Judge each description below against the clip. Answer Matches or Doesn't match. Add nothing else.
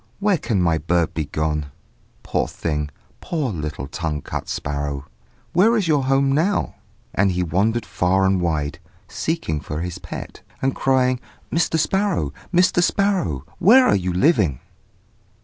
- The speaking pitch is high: Doesn't match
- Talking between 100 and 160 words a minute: Matches